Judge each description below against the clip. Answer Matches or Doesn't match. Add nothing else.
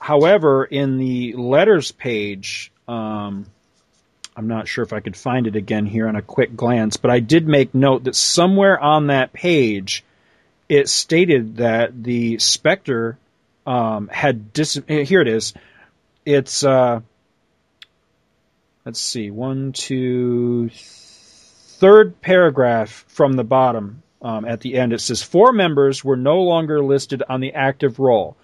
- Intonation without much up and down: Doesn't match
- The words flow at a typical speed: Matches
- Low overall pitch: Matches